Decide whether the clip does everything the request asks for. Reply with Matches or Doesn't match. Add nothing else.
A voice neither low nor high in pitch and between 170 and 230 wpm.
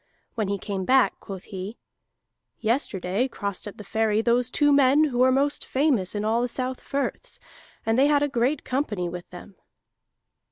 Doesn't match